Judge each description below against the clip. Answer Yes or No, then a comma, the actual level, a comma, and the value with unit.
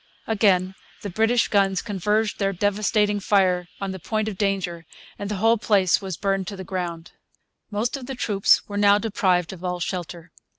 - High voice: Yes, high, 195 Hz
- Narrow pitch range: Yes, narrow, 2.3 semitones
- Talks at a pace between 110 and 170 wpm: No, average, 180 wpm